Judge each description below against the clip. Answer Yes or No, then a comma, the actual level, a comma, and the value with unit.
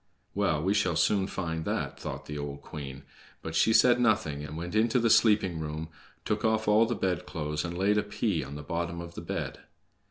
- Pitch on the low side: Yes, very low, 85 Hz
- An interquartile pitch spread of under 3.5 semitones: No, wide, 5.6 semitones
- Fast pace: Yes, fast, 210 wpm